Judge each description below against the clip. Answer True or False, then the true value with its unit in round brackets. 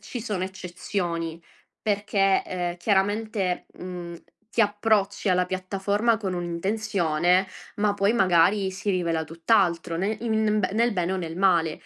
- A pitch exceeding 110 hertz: True (190 Hz)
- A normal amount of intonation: True (3.0 semitones)